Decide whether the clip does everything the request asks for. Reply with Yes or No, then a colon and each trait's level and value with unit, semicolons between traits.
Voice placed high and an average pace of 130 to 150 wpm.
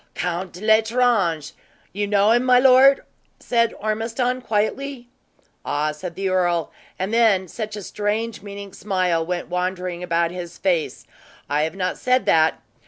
Yes: high, 200 Hz; average, 145 wpm